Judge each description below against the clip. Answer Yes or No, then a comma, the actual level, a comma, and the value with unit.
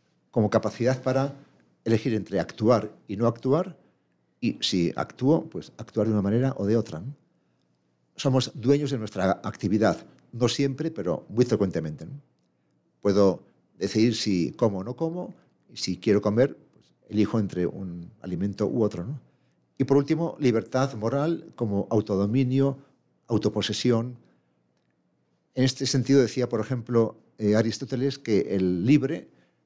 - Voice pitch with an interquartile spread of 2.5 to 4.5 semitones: No, average, 5.1 semitones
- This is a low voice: Yes, low, 115 Hz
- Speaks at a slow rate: No, average, 140 wpm